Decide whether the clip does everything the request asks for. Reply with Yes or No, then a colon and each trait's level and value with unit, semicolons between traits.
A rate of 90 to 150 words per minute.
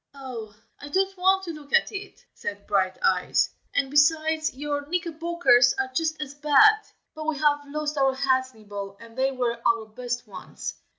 No: average, 170 wpm